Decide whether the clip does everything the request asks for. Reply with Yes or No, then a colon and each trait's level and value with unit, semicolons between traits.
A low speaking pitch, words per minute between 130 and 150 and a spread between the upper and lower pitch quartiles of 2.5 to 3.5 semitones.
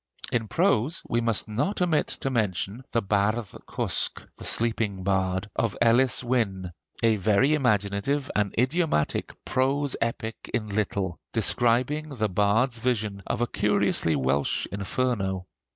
No: low, 115 Hz; slow, 135 wpm; average, 4.2 semitones